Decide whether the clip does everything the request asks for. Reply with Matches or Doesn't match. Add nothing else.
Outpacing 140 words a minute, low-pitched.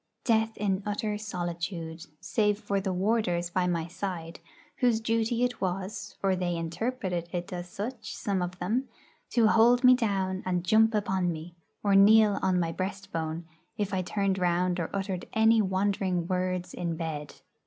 Doesn't match